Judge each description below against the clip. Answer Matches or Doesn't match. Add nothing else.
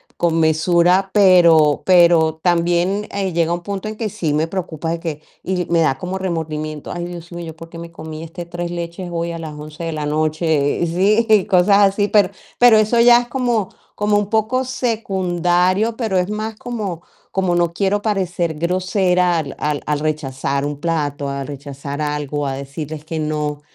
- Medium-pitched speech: Matches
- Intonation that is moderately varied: Matches